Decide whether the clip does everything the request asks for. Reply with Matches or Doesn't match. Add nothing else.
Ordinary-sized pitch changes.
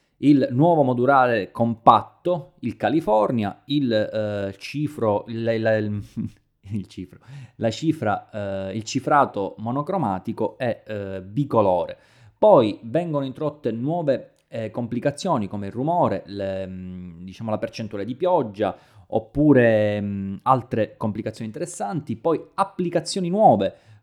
Doesn't match